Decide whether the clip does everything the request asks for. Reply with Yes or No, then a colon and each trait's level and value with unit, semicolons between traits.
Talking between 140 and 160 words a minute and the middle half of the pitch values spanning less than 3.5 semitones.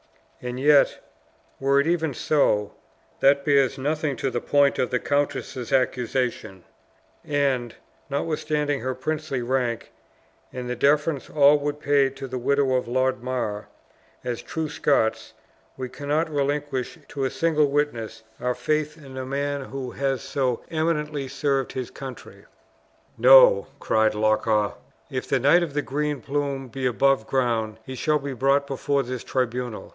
Yes: average, 150 wpm; narrow, 2.5 semitones